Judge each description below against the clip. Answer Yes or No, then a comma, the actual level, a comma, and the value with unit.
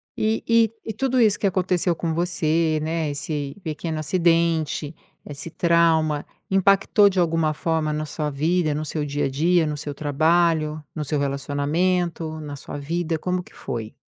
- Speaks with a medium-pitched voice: Yes, medium, 160 Hz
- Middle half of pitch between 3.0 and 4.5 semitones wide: No, narrow, 2.6 semitones